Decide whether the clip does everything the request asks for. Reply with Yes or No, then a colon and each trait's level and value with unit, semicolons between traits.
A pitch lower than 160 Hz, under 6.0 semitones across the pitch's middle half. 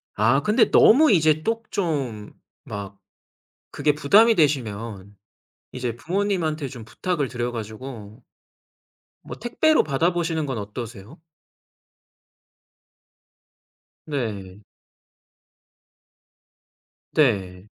No: low, 135 Hz; wide, 7.1 semitones